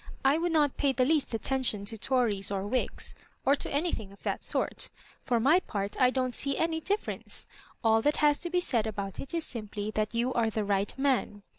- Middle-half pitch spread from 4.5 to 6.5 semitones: Yes, average, 5.2 semitones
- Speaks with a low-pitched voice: No, very high, 250 Hz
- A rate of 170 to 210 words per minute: Yes, fast, 205 wpm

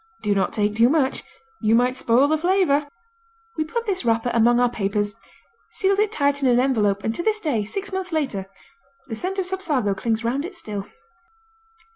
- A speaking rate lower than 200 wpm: Yes, average, 190 wpm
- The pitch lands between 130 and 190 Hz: No, very high, 260 Hz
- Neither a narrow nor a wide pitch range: No, wide, 7.7 semitones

